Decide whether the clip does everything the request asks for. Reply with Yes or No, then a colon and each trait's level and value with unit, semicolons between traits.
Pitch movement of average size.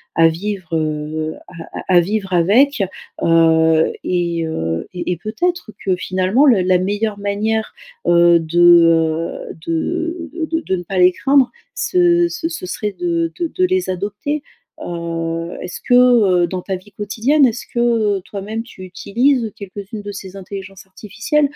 No: wide, 5.7 semitones